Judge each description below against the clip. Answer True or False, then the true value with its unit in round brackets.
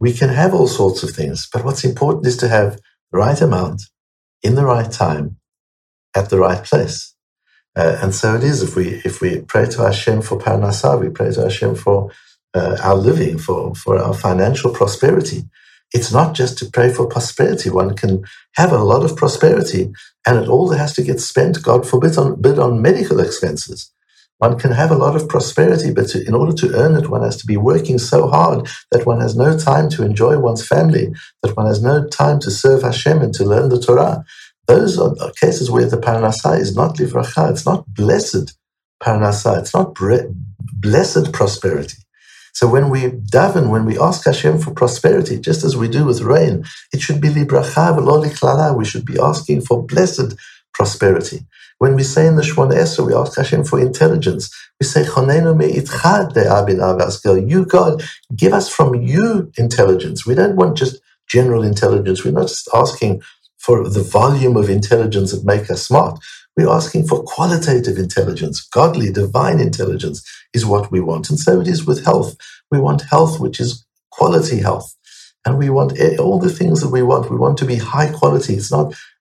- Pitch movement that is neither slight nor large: False (5.9 semitones)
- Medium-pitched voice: False (120 Hz)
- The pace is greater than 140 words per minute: True (190 wpm)